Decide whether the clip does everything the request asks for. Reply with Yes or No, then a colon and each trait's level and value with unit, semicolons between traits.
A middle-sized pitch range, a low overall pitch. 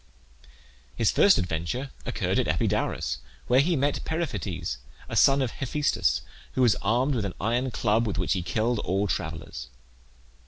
No: wide, 6.3 semitones; low, 115 Hz